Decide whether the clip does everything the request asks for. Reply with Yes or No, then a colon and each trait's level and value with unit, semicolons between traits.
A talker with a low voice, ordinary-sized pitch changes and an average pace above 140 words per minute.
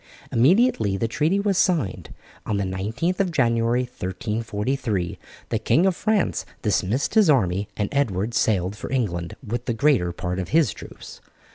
No: low, 115 Hz; wide, 7.3 semitones; average, 155 wpm